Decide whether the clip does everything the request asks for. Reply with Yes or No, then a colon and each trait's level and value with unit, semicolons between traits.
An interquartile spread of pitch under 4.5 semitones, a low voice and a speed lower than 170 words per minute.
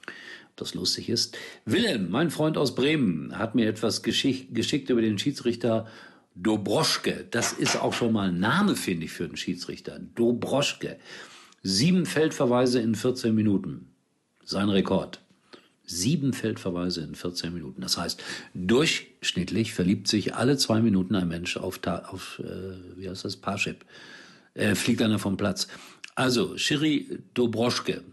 No: average, 4.8 semitones; low, 115 Hz; average, 145 wpm